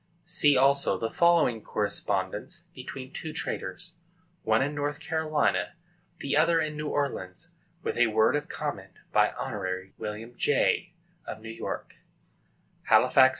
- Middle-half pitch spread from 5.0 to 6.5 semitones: Yes, wide, 5.5 semitones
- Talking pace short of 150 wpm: Yes, average, 140 wpm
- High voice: No, low, 135 Hz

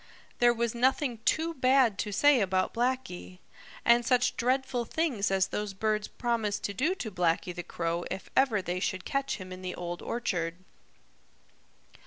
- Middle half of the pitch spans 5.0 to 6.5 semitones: Yes, wide, 5.4 semitones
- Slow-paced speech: No, average, 165 wpm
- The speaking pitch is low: No, high, 220 Hz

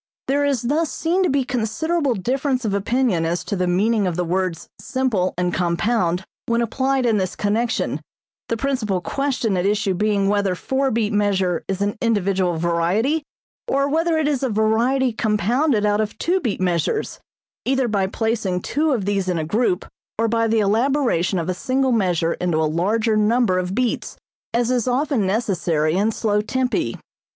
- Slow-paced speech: No, average, 180 wpm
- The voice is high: Yes, high, 215 Hz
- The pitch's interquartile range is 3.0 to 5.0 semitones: No, wide, 5.5 semitones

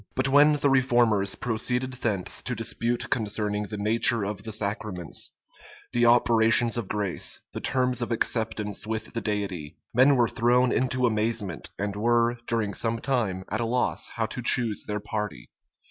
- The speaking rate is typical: Yes, average, 160 wpm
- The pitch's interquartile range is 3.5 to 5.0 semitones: No, narrow, 2.6 semitones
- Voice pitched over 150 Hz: No, low, 115 Hz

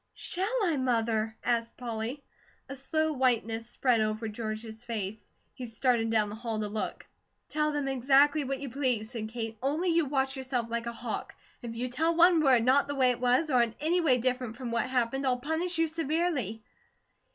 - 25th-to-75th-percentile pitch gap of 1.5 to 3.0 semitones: No, average, 3.9 semitones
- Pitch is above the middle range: Yes, very high, 250 Hz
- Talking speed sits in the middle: Yes, average, 195 wpm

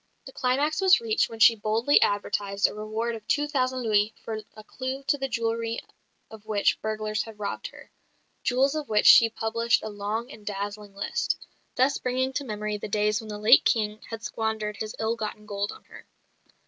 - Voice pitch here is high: Yes, high, 220 Hz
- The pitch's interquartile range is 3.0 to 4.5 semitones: Yes, average, 3.3 semitones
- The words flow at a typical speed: Yes, average, 195 wpm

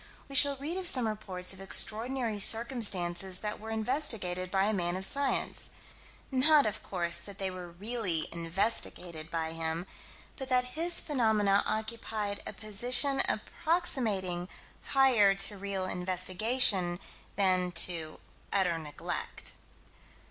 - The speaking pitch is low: No, high, 200 Hz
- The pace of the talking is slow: Yes, slow, 125 wpm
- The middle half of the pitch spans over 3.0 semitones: Yes, average, 5.2 semitones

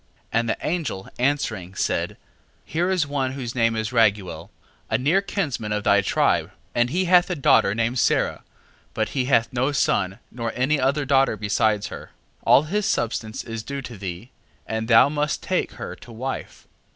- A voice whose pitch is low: Yes, low, 120 Hz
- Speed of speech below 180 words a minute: No, average, 185 wpm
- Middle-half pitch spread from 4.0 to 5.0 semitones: Yes, average, 4.5 semitones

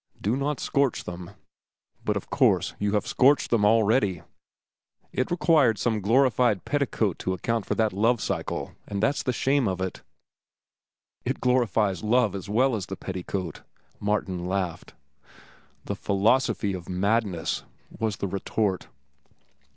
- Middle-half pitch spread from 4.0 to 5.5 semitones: Yes, average, 4.4 semitones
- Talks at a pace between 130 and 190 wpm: Yes, average, 140 wpm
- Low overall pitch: Yes, low, 105 Hz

